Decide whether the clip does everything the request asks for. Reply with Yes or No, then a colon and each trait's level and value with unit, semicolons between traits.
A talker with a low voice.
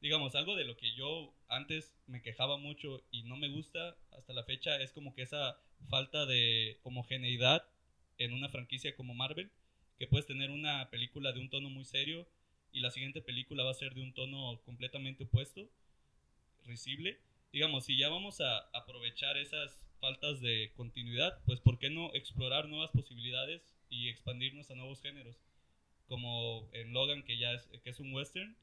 Yes: low, 130 Hz